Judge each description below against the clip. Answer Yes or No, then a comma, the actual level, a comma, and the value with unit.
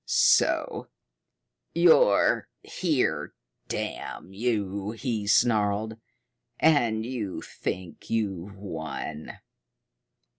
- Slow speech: Yes, slow, 70 wpm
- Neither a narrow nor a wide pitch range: Yes, average, 3.1 semitones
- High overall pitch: No, low, 105 Hz